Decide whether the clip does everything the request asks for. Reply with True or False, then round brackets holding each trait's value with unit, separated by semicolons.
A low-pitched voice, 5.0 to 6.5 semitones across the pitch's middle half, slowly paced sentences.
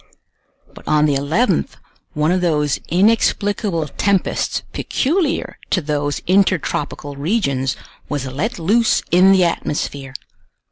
False (165 Hz; 5.4 semitones; 110 wpm)